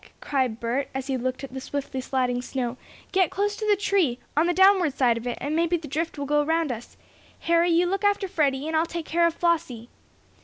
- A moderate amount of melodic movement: Yes, average, 4.8 semitones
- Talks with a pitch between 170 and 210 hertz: No, very high, 305 Hz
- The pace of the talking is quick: Yes, fast, 230 wpm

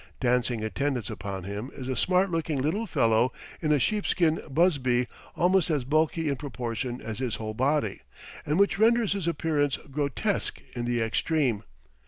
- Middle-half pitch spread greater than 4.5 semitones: Yes, average, 5.2 semitones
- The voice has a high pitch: No, medium, 140 Hz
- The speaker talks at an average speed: Yes, average, 160 wpm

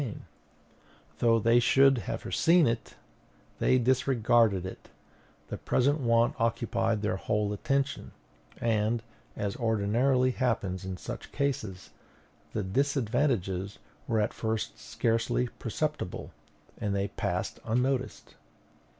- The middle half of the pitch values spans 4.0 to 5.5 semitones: No, average, 3.6 semitones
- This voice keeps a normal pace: No, slow, 110 wpm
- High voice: No, low, 115 Hz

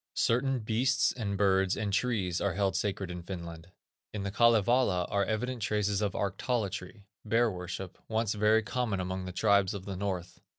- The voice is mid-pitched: No, low, 100 Hz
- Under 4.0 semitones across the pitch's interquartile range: Yes, average, 2.9 semitones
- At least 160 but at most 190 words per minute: Yes, average, 170 wpm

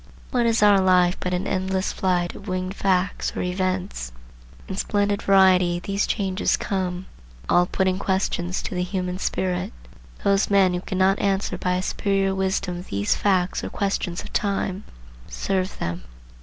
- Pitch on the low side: No, high, 190 Hz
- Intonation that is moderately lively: No, narrow, 1.4 semitones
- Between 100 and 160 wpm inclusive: Yes, average, 155 wpm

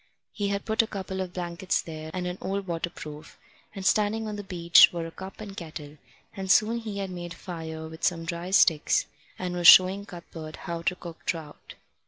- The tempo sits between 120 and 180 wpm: No, fast, 205 wpm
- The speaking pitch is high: No, medium, 180 Hz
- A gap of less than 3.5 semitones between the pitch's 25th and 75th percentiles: Yes, average, 2.8 semitones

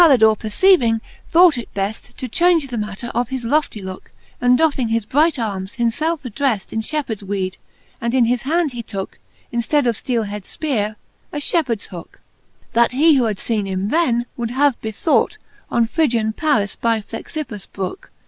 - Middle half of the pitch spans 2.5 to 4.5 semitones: No, average, 5.0 semitones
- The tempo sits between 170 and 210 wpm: Yes, average, 175 wpm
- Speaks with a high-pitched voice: Yes, high, 235 Hz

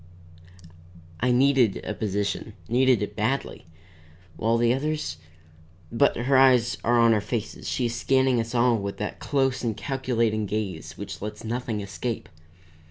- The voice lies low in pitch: Yes, low, 115 Hz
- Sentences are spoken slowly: No, average, 150 wpm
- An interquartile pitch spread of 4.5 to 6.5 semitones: No, average, 3.3 semitones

